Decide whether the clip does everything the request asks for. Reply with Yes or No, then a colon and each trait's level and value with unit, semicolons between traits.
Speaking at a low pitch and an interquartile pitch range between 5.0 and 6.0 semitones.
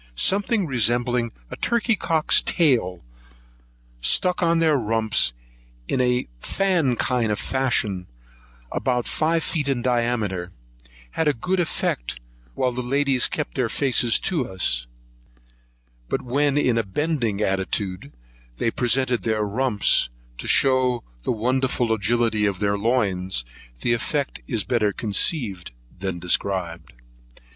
Yes: low, 120 Hz; average, 5.3 semitones